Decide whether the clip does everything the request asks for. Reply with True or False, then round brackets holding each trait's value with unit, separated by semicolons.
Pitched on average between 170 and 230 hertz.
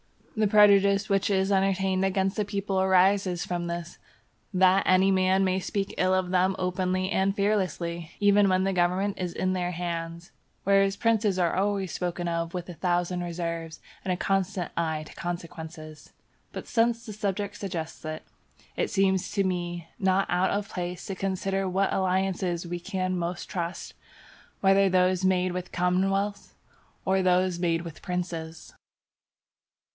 True (185 Hz)